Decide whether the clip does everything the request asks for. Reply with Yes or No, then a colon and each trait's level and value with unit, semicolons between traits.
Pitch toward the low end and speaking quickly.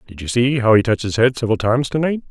Yes: low, 120 Hz; fast, 315 wpm